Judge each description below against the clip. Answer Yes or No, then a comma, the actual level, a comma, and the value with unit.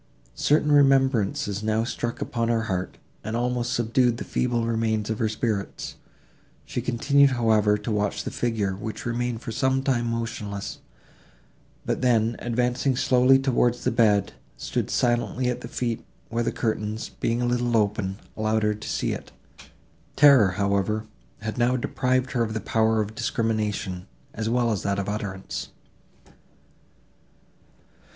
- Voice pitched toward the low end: Yes, low, 115 Hz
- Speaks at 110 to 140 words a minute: No, average, 155 wpm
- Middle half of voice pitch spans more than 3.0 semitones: No, narrow, 2.4 semitones